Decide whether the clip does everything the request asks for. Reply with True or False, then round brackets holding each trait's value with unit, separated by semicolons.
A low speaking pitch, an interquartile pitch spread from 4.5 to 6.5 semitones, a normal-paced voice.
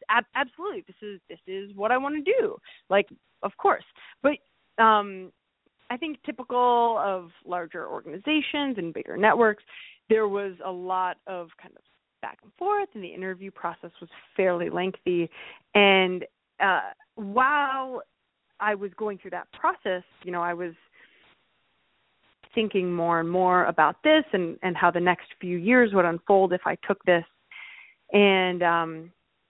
False (195 Hz; 5.5 semitones; 155 wpm)